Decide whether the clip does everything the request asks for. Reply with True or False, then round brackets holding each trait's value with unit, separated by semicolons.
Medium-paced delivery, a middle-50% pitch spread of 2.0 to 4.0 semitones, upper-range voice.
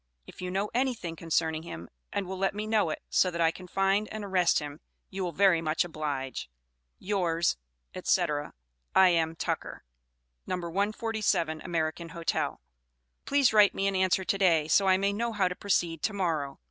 False (175 wpm; 3.4 semitones; 180 Hz)